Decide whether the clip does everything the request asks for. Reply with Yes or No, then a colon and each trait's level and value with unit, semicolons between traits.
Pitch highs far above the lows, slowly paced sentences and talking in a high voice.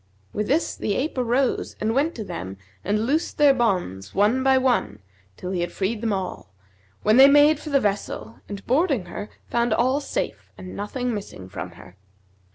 No: wide, 5.9 semitones; average, 190 wpm; high, 225 Hz